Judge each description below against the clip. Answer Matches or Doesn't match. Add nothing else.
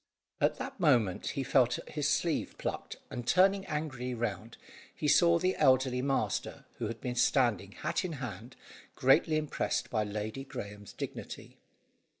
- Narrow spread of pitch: Doesn't match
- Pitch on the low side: Matches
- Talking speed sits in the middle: Matches